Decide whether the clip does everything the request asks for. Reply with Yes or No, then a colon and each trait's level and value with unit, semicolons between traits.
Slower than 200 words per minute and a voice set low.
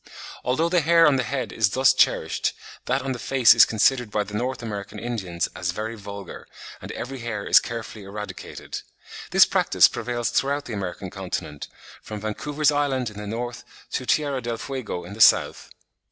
Yes: average, 180 wpm; low, 115 Hz